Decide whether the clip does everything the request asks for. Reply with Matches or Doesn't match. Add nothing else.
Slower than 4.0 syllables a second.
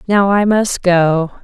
Matches